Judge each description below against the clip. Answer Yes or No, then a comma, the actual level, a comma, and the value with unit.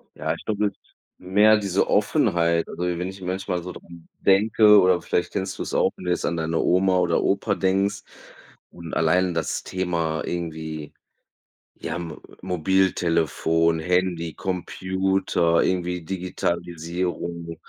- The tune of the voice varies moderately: No, narrow, 2.2 semitones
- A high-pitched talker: No, very low, 90 Hz